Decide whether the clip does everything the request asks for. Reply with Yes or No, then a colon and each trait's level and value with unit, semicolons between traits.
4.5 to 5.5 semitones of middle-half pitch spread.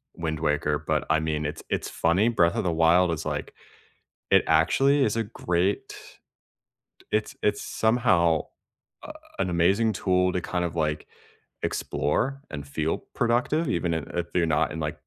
Yes: average, 5.0 semitones